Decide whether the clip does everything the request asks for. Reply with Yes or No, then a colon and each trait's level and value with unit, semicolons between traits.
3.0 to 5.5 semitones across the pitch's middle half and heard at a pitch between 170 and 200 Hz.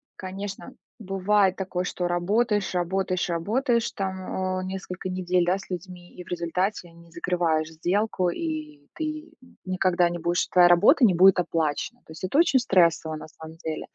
No: narrow, 2.4 semitones; medium, 185 Hz